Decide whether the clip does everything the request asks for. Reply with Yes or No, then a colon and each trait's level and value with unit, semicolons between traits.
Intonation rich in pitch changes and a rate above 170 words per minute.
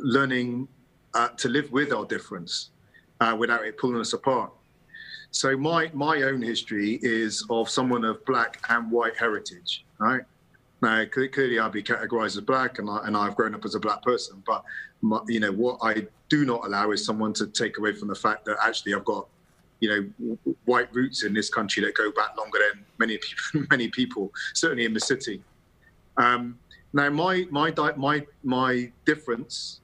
No: average, 3.5 semitones; average, 190 wpm